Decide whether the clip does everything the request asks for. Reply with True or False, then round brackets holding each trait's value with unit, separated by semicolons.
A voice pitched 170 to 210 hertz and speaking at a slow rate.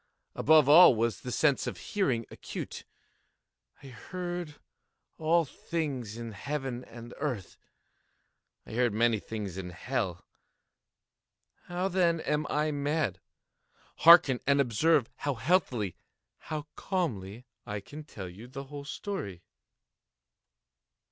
False (135 Hz; 120 wpm)